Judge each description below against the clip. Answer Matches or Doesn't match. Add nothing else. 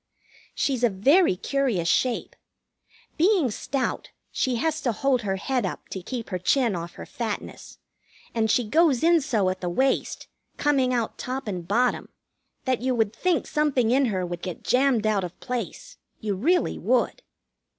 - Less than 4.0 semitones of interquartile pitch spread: Doesn't match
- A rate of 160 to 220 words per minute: Matches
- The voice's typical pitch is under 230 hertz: Doesn't match